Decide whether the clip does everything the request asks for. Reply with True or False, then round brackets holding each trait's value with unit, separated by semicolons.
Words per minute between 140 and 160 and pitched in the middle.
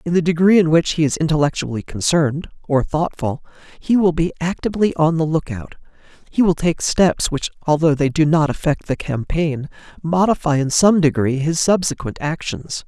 False (170 wpm; 160 Hz)